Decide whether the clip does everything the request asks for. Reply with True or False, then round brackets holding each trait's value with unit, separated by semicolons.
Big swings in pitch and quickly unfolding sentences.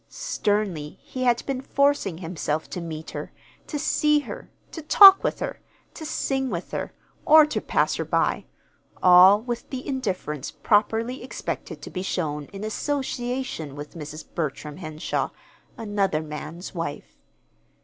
False (8.6 semitones; 145 wpm)